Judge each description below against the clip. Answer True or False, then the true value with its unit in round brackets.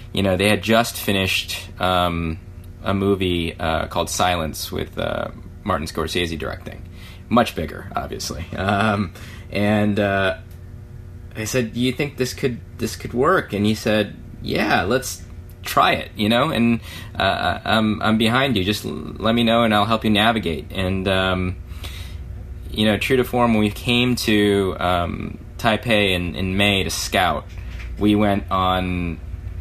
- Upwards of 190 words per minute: False (160 wpm)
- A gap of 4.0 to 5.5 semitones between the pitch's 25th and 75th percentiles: False (3.3 semitones)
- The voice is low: True (95 Hz)